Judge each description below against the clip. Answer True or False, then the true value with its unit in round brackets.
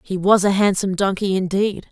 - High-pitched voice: True (195 Hz)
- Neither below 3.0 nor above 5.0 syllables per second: False (5.5 syllables/s)